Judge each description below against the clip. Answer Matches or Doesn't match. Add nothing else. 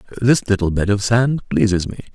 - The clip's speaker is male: Matches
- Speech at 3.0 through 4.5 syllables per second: Doesn't match